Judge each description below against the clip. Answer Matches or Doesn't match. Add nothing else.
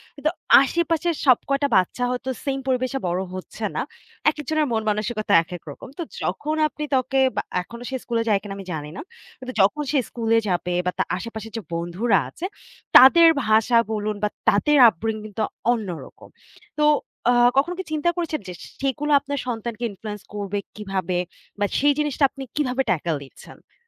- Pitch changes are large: Matches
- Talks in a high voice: Matches